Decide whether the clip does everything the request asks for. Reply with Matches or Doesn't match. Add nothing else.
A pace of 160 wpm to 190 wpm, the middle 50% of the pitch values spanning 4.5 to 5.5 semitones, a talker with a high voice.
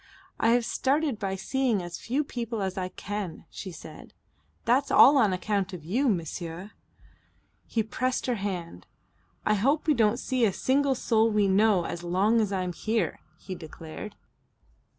Matches